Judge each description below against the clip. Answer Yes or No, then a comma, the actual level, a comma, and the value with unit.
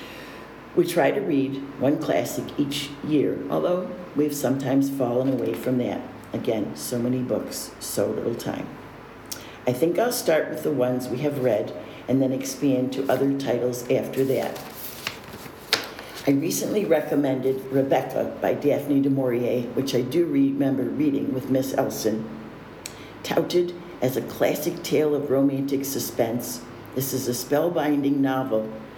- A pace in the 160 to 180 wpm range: No, average, 145 wpm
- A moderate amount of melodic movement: No, narrow, 2.3 semitones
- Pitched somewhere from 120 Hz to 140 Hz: Yes, low, 135 Hz